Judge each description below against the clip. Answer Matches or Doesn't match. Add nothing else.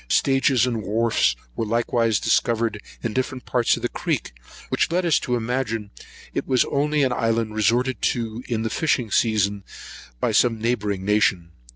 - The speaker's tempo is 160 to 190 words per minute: Matches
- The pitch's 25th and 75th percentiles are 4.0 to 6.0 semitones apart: Doesn't match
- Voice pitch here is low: Matches